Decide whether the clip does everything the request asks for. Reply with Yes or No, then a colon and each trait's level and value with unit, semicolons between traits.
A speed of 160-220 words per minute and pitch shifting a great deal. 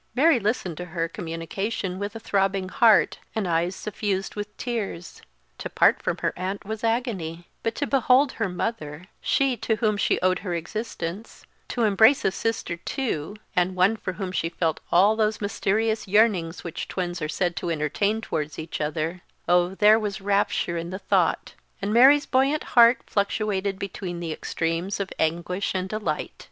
No: average, 170 wpm; average, 4.0 semitones